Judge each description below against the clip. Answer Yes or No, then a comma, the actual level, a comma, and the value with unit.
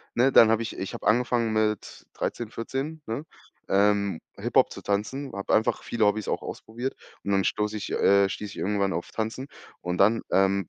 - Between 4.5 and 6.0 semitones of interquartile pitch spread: No, average, 2.8 semitones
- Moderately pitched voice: No, low, 105 Hz